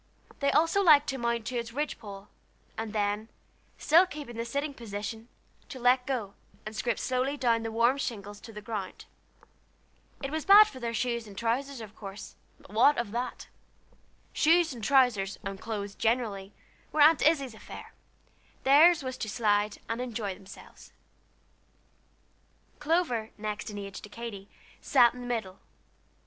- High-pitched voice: Yes, high, 235 Hz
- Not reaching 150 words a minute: No, average, 160 wpm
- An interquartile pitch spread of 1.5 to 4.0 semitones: No, average, 4.5 semitones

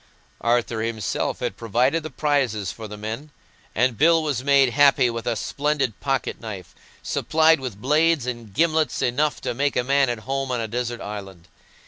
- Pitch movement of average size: Yes, average, 4.3 semitones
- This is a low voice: Yes, low, 125 Hz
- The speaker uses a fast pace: No, average, 175 wpm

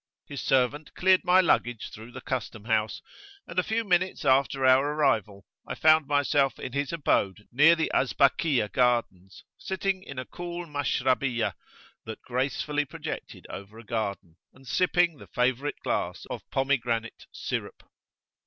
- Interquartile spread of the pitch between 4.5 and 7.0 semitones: Yes, average, 4.9 semitones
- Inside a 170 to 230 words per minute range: No, average, 145 wpm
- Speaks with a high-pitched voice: No, low, 135 Hz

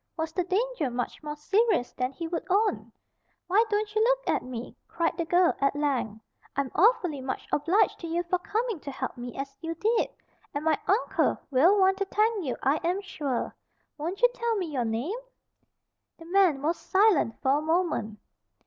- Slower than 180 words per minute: No, average, 190 wpm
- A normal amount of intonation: No, wide, 6.3 semitones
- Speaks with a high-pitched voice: Yes, very high, 335 Hz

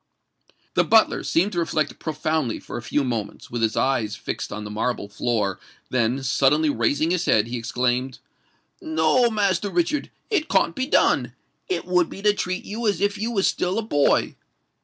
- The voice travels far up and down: Yes, wide, 8.6 semitones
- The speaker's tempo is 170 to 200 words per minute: Yes, average, 180 wpm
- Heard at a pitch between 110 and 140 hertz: No, medium, 155 Hz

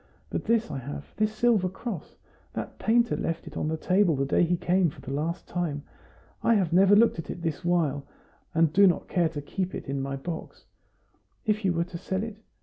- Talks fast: Yes, fast, 225 wpm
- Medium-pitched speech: Yes, medium, 175 Hz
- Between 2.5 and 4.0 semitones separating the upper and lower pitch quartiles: No, average, 4.5 semitones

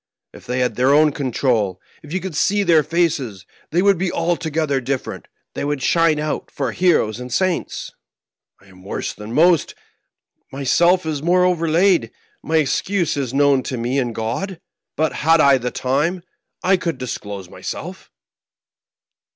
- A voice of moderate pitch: Yes, medium, 150 Hz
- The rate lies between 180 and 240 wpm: No, average, 160 wpm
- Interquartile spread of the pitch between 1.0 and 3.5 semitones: No, average, 5.3 semitones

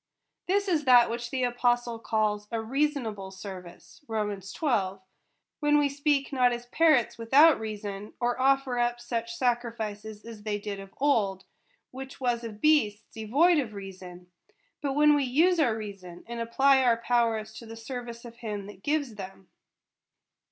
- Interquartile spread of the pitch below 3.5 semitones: No, average, 4.3 semitones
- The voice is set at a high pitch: Yes, high, 235 Hz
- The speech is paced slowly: No, average, 165 wpm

